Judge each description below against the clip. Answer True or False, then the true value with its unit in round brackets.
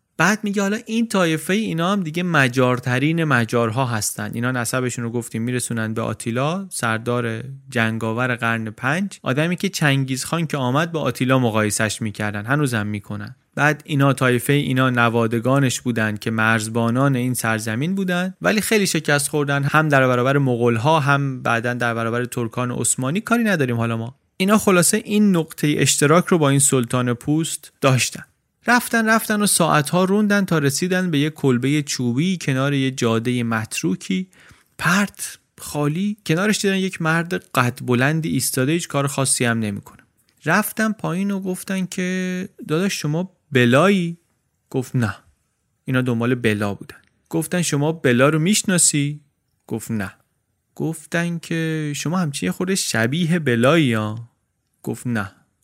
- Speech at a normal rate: True (145 wpm)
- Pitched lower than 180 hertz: True (140 Hz)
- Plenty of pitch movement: True (6.4 semitones)